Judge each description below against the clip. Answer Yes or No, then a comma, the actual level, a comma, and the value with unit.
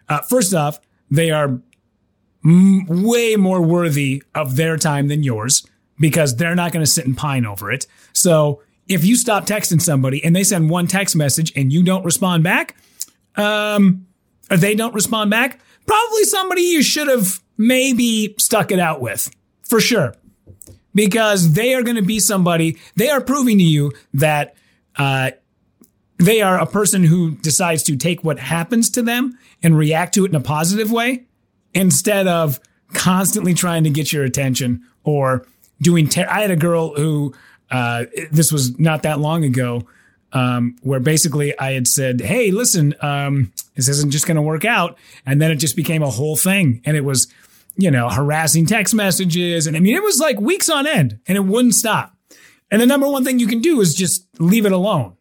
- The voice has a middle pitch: Yes, medium, 165 Hz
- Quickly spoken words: No, average, 190 wpm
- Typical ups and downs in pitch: No, wide, 6.3 semitones